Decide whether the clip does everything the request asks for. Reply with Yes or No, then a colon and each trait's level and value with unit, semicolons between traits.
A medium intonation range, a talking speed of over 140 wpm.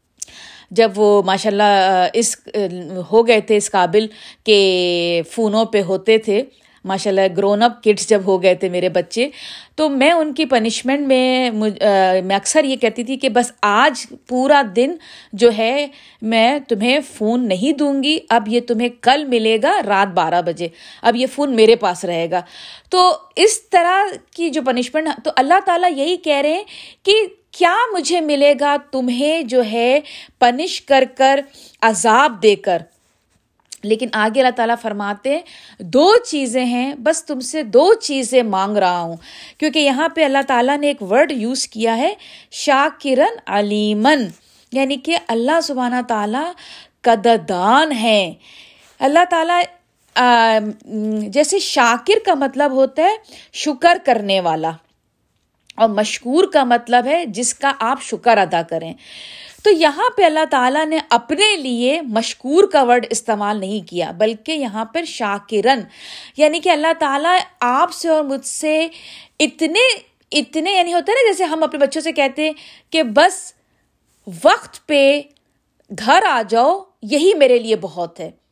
No: wide, 6.0 semitones; average, 155 wpm